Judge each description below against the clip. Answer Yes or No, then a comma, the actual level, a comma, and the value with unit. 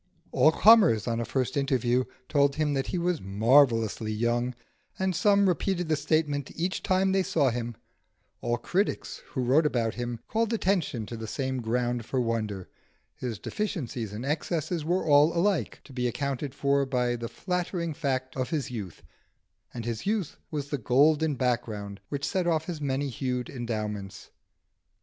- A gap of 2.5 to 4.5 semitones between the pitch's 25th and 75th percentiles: No, average, 5.2 semitones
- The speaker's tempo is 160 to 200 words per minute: Yes, average, 165 wpm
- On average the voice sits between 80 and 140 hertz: Yes, low, 135 Hz